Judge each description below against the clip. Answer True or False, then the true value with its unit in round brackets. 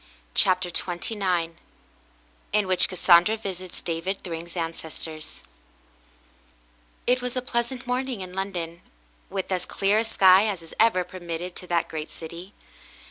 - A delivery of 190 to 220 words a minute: False (135 wpm)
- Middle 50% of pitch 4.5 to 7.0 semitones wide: False (3.3 semitones)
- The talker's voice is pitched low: False (185 Hz)